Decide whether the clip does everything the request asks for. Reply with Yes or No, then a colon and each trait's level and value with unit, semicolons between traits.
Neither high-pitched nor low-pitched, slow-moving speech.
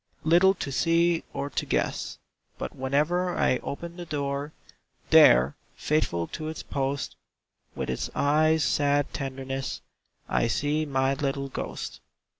Yes: medium, 145 Hz; slow, 130 wpm